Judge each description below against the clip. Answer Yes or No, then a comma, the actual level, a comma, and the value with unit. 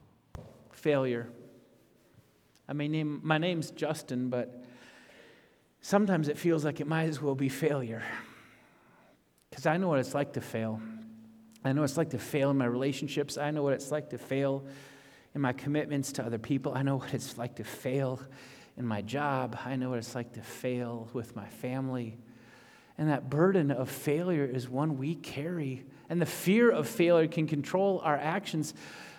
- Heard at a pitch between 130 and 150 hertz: Yes, low, 135 Hz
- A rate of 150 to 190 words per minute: Yes, average, 180 wpm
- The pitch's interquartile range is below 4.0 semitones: Yes, average, 3.6 semitones